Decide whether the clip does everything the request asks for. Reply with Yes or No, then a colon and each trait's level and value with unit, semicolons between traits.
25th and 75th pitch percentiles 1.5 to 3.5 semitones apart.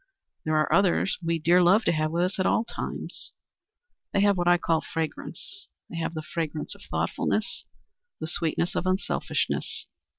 Yes: narrow, 2.6 semitones